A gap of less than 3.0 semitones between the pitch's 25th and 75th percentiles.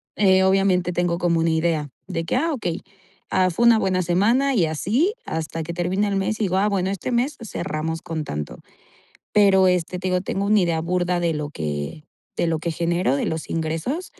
No: average, 3.3 semitones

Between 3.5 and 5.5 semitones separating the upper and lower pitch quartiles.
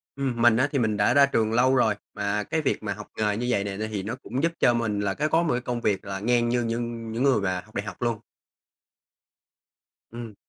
No: average, 2.8 semitones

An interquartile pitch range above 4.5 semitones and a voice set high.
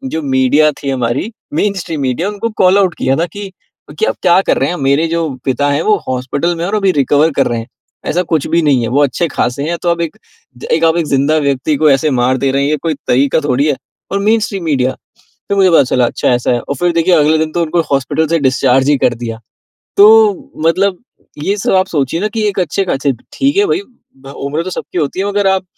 No: average, 5.2 semitones; medium, 155 Hz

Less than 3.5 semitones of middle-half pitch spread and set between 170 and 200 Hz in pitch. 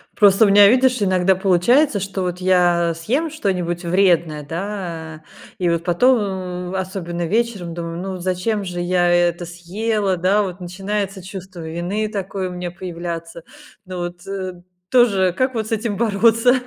Yes: average, 2.8 semitones; medium, 185 Hz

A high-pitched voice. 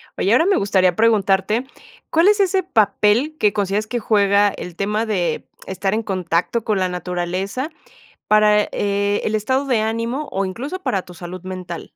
Yes: high, 205 Hz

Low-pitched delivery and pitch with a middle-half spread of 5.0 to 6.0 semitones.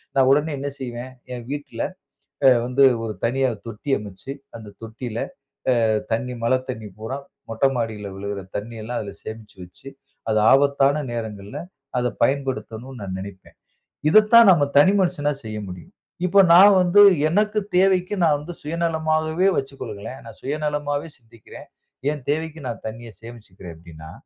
Yes: low, 130 Hz; wide, 5.5 semitones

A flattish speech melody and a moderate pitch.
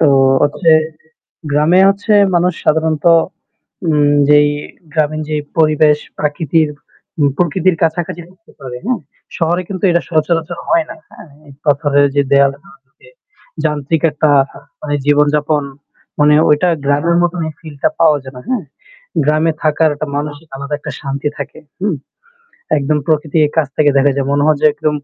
Yes: narrow, 2.1 semitones; medium, 155 Hz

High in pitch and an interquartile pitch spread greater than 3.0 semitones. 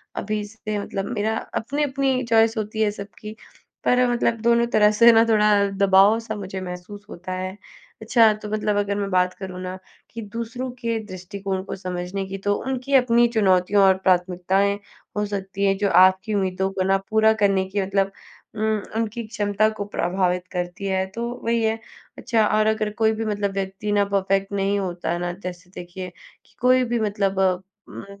No: high, 200 Hz; narrow, 2.6 semitones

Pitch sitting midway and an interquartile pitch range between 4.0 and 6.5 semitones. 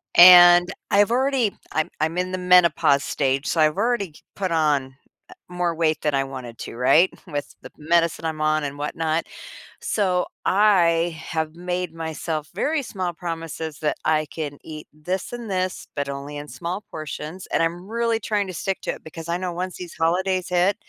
No: medium, 170 Hz; average, 3.1 semitones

